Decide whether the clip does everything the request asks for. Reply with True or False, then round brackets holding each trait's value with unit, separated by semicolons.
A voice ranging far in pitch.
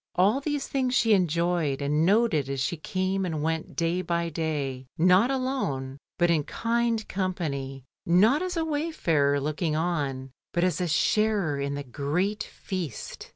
True (6.5 semitones)